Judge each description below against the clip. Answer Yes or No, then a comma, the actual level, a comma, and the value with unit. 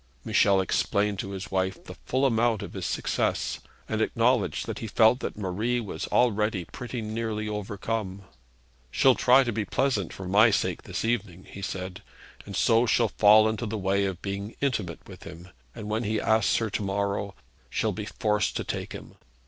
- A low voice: Yes, low, 105 Hz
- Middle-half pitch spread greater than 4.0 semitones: No, narrow, 2.5 semitones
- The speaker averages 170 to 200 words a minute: Yes, average, 185 wpm